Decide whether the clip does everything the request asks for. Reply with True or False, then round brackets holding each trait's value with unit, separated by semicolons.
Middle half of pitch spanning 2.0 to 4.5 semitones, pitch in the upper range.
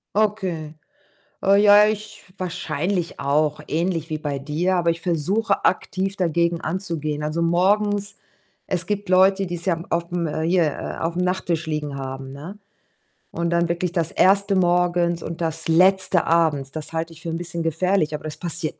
False (2.7 semitones; 170 Hz)